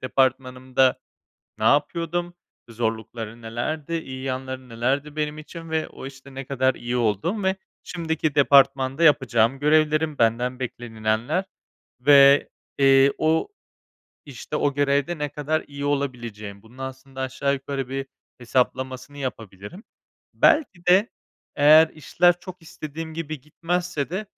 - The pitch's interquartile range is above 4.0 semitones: No, average, 3.5 semitones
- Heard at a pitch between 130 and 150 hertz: Yes, medium, 140 Hz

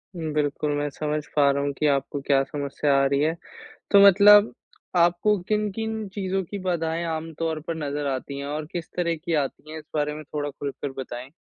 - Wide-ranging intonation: No, average, 3.4 semitones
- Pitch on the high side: No, medium, 155 Hz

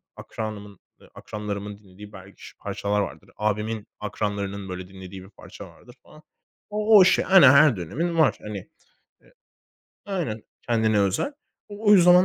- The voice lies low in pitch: Yes, low, 105 Hz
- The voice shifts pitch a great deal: Yes, wide, 7.6 semitones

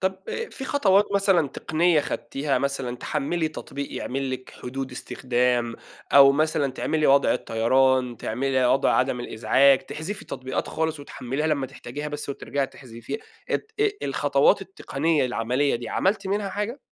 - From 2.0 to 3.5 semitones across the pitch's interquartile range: No, average, 4.5 semitones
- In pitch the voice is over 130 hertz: Yes, medium, 140 Hz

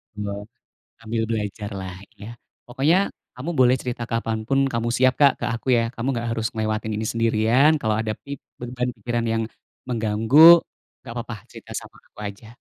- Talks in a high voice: No, low, 115 Hz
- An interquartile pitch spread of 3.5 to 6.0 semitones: No, narrow, 2.5 semitones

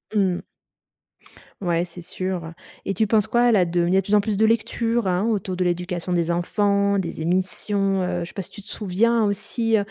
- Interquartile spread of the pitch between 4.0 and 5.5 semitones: No, average, 2.9 semitones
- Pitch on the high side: Yes, high, 195 Hz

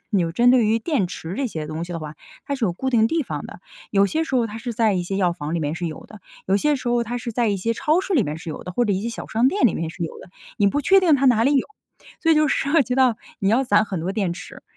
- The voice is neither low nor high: No, high, 225 Hz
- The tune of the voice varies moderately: No, wide, 6.3 semitones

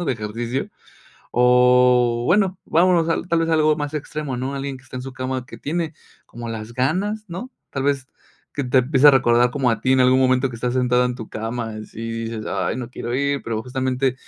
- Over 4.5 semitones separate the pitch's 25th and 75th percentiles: No, average, 2.7 semitones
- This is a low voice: Yes, low, 130 Hz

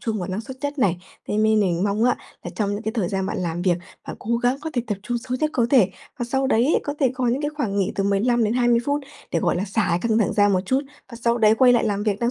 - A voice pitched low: No, high, 225 Hz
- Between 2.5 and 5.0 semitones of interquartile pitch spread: Yes, average, 3.8 semitones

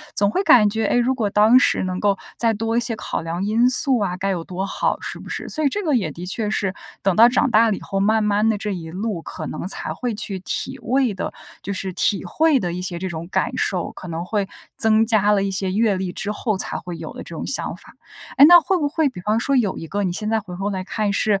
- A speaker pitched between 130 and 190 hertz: No, high, 205 Hz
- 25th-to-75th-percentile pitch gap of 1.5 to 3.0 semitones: No, average, 3.5 semitones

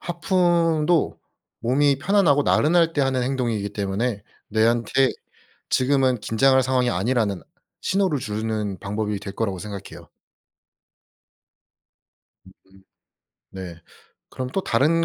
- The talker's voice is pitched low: Yes, low, 125 Hz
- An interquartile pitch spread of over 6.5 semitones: No, wide, 5.9 semitones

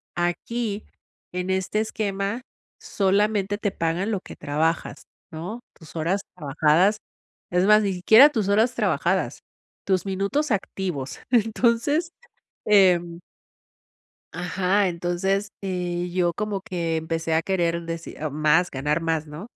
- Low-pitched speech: No, medium, 185 Hz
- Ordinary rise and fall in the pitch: Yes, average, 3.5 semitones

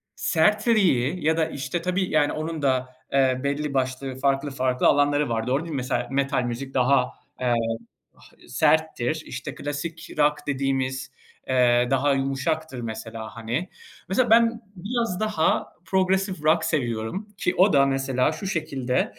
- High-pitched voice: No, medium, 140 Hz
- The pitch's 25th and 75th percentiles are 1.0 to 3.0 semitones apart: No, average, 4.2 semitones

